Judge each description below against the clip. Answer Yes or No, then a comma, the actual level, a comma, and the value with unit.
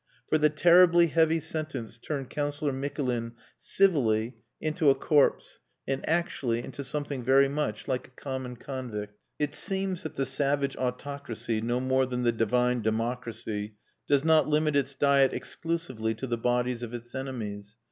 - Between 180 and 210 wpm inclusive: No, average, 155 wpm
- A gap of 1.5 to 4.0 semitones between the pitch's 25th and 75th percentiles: Yes, average, 3.7 semitones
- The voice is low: Yes, low, 130 Hz